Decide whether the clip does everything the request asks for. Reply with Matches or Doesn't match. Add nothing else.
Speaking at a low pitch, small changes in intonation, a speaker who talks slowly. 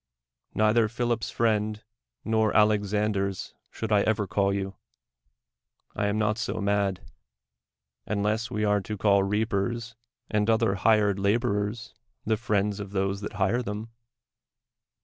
Matches